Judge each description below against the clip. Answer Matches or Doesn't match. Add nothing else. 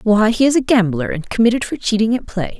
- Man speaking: Doesn't match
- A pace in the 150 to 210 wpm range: Doesn't match